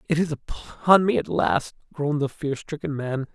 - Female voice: No, male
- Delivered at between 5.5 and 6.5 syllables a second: No, 4.8 syllables/s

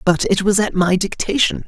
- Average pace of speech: No, fast, 215 wpm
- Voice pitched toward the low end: No, high, 190 Hz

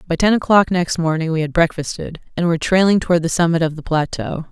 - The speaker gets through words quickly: Yes, fast, 225 wpm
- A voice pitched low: No, medium, 165 Hz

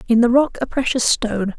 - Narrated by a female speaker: Yes, female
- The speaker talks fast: Yes, fast, 225 wpm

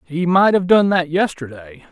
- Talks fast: No, average, 190 wpm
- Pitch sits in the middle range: Yes, medium, 170 Hz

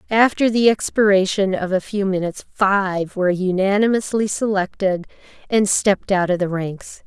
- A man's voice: No, female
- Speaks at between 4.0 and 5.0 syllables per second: Yes, 4.9 syllables/s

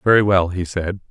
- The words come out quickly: Yes, fast, 215 wpm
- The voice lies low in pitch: Yes, very low, 95 Hz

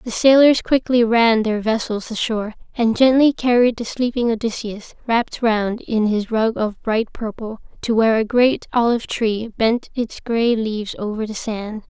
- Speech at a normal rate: Yes, average, 170 wpm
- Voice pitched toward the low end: No, high, 230 Hz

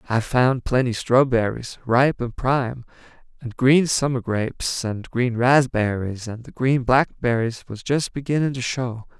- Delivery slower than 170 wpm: Yes, average, 150 wpm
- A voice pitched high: No, low, 125 Hz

